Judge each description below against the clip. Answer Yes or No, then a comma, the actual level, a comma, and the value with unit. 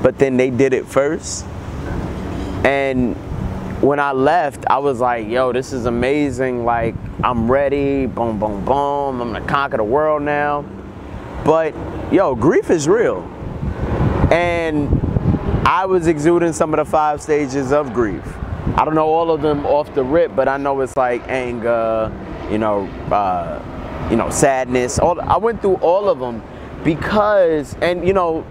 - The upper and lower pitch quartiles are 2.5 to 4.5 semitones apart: No, average, 4.9 semitones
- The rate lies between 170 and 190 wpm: No, average, 160 wpm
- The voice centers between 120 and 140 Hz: Yes, low, 135 Hz